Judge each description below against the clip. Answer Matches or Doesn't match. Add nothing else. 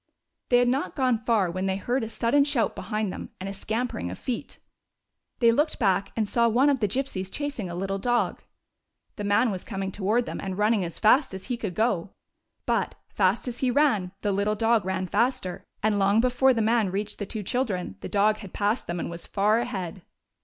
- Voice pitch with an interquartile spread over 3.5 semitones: Matches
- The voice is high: Matches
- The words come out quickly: Matches